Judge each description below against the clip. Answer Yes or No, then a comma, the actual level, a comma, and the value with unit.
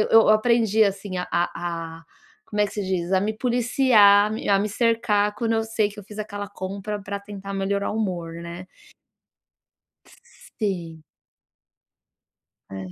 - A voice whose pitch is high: Yes, high, 205 Hz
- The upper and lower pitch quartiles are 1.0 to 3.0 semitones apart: Yes, narrow, 2.6 semitones